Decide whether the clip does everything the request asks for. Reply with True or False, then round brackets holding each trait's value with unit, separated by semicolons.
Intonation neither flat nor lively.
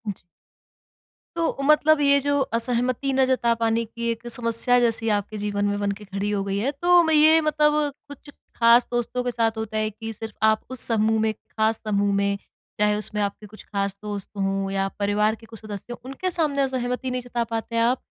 True (3.3 semitones)